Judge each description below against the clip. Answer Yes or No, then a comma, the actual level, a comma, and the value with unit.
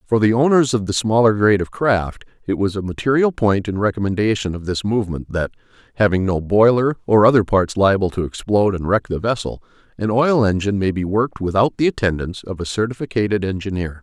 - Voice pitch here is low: Yes, low, 105 Hz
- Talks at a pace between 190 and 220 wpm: Yes, average, 195 wpm